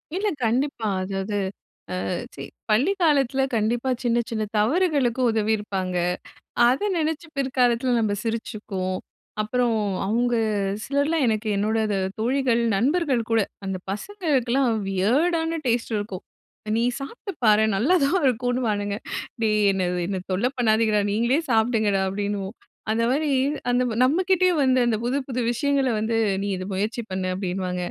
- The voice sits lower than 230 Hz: No, high, 235 Hz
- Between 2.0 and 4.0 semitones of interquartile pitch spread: No, average, 4.5 semitones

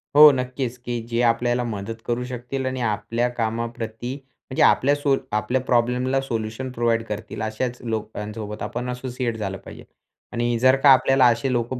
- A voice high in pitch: No, low, 120 Hz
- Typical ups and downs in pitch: No, narrow, 2.2 semitones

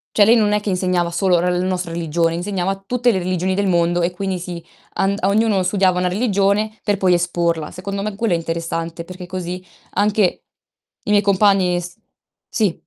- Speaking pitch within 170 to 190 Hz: Yes, medium, 185 Hz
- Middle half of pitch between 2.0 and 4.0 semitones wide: Yes, narrow, 2.4 semitones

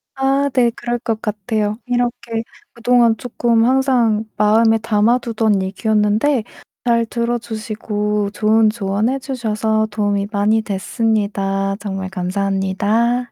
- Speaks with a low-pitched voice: No, high, 220 Hz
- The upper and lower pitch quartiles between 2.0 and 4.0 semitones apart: Yes, narrow, 2.4 semitones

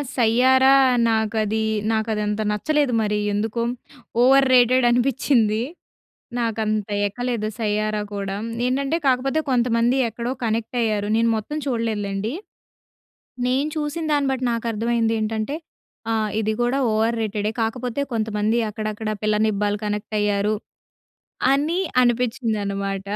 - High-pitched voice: Yes, high, 225 Hz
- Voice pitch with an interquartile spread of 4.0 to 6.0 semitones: No, average, 2.9 semitones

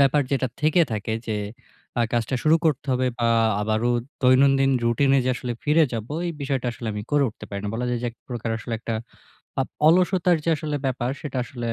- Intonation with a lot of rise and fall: No, average, 3.8 semitones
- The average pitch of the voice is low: Yes, low, 130 Hz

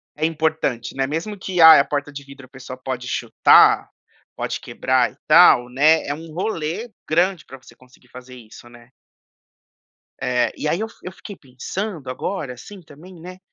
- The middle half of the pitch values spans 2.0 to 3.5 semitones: No, average, 5.0 semitones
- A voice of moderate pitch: Yes, medium, 145 Hz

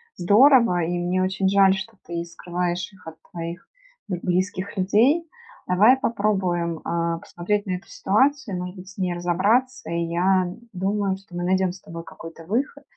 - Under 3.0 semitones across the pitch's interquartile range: Yes, narrow, 2.6 semitones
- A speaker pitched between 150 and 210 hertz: Yes, medium, 185 Hz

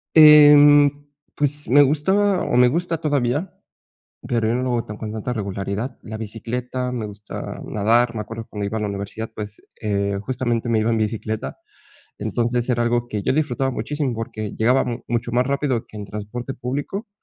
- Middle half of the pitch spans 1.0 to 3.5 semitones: No, average, 4.1 semitones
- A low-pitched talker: Yes, low, 120 Hz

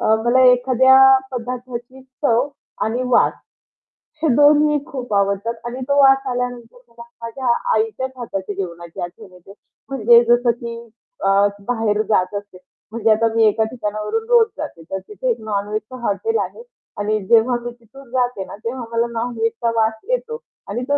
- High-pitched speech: Yes, high, 235 Hz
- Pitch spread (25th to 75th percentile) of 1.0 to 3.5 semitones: Yes, average, 3.2 semitones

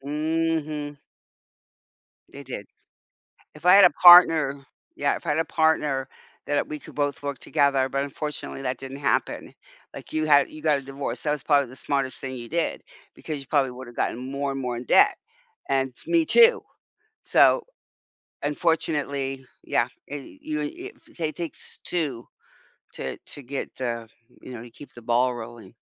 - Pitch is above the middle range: No, medium, 140 Hz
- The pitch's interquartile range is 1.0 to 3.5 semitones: Yes, average, 2.9 semitones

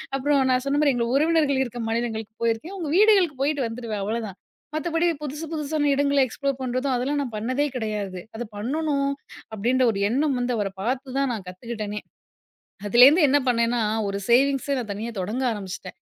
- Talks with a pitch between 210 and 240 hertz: No, very high, 255 Hz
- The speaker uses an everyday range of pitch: Yes, average, 4.1 semitones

